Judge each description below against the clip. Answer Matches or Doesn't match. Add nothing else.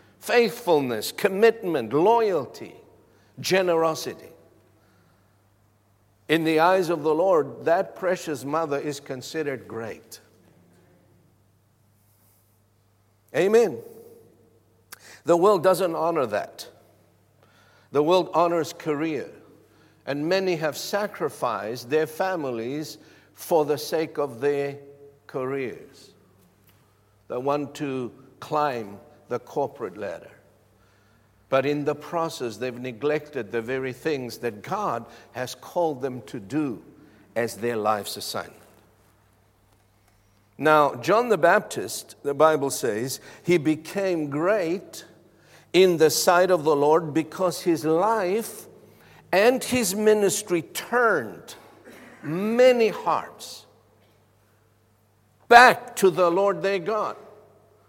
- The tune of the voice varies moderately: Doesn't match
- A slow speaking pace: Matches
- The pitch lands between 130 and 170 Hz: Matches